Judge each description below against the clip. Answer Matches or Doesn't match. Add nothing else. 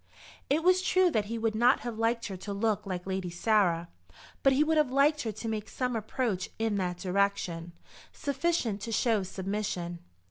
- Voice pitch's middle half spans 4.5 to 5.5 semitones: Matches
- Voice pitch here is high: Matches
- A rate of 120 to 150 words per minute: Doesn't match